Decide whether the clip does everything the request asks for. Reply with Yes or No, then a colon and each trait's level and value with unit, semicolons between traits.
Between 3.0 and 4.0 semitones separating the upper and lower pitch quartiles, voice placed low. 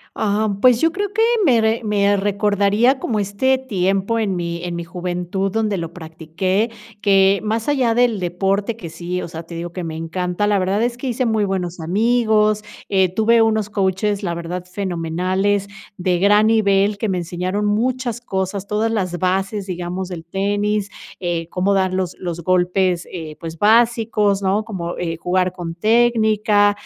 No: average, 3.3 semitones; high, 195 Hz